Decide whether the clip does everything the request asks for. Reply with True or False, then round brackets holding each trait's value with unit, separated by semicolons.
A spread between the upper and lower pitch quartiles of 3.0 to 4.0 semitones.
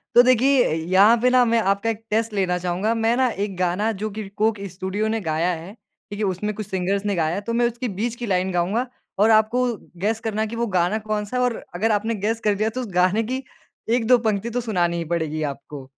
True (3.5 semitones)